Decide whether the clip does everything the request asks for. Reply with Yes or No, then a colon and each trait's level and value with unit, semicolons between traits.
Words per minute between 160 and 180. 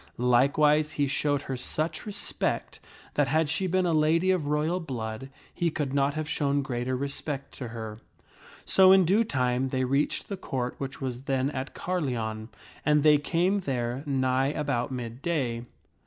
Yes: average, 170 wpm